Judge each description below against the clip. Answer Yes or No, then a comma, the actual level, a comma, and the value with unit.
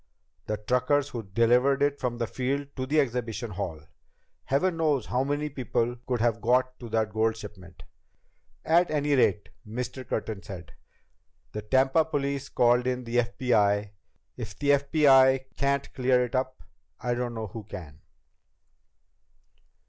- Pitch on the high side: No, low, 125 Hz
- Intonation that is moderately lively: Yes, average, 3.7 semitones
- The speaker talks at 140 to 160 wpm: Yes, average, 150 wpm